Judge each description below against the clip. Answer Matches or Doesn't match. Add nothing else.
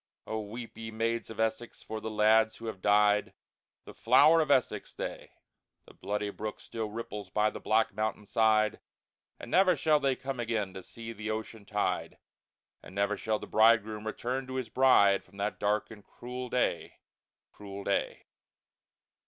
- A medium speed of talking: Matches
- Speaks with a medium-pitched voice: Doesn't match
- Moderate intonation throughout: Doesn't match